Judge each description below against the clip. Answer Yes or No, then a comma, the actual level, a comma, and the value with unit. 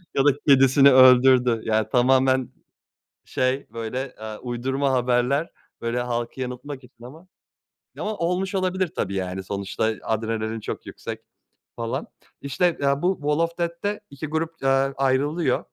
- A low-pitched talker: Yes, low, 130 Hz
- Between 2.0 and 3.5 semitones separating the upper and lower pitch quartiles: No, average, 4.0 semitones